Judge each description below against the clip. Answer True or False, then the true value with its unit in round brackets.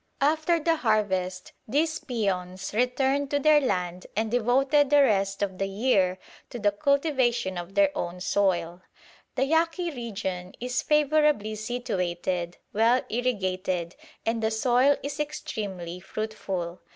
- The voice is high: True (220 Hz)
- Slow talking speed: True (130 wpm)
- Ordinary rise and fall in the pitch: False (6.9 semitones)